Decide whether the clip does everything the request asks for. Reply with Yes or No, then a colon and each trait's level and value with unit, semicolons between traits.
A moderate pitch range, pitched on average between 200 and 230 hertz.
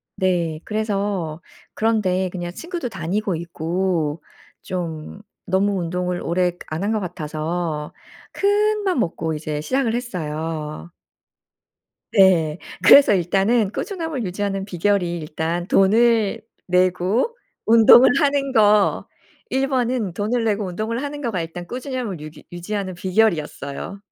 No: average, 4.7 semitones; high, 190 Hz